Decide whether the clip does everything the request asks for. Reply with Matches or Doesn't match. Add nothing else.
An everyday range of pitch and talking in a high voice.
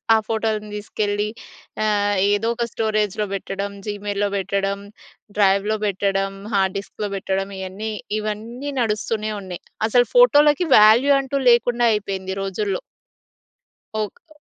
Doesn't match